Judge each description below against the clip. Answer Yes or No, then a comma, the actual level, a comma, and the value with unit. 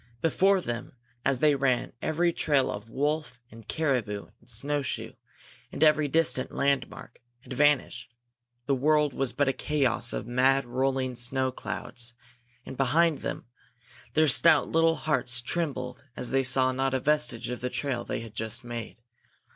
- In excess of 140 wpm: Yes, average, 160 wpm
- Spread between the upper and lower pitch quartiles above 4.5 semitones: No, average, 3.5 semitones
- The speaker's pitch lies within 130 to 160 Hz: Yes, low, 135 Hz